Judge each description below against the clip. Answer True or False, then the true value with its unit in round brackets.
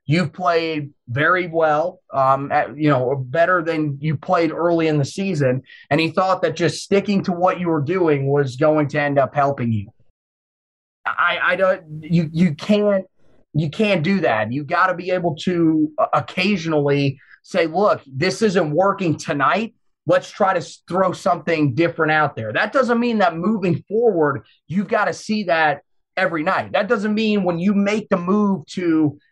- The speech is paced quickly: False (180 wpm)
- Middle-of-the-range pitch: True (170 Hz)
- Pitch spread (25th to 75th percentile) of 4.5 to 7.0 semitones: False (4.1 semitones)